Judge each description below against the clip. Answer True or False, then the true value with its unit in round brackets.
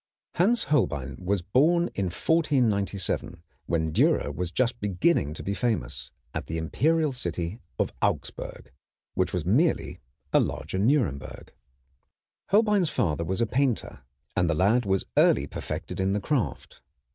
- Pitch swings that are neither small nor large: False (8.2 semitones)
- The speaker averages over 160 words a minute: False (140 wpm)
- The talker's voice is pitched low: True (100 Hz)